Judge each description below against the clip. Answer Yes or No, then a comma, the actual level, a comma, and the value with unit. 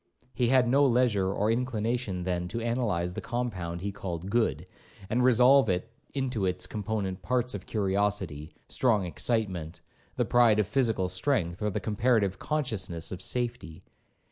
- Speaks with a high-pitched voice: No, low, 105 Hz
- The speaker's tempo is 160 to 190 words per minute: No, average, 150 wpm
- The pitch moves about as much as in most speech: Yes, average, 4.8 semitones